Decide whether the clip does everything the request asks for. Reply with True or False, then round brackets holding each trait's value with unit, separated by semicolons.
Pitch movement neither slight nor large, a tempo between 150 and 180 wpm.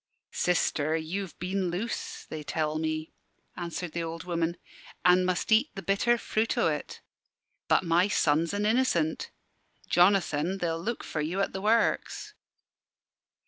False (3.4 semitones; 140 wpm)